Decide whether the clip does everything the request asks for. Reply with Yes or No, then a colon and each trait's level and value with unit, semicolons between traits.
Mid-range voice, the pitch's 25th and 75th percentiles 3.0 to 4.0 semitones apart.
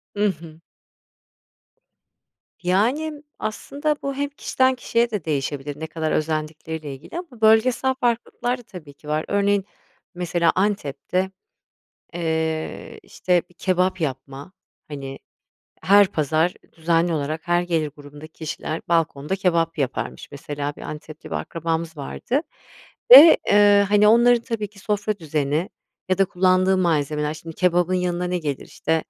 No: medium, 175 Hz; average, 4.9 semitones